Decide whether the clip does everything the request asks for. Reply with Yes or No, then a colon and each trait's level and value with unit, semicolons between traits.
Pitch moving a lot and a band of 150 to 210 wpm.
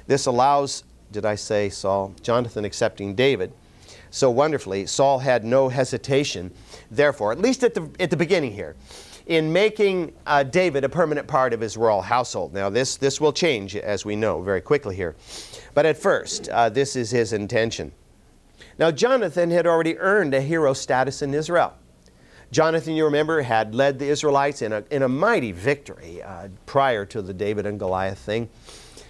Yes: wide, 6.1 semitones; average, 175 wpm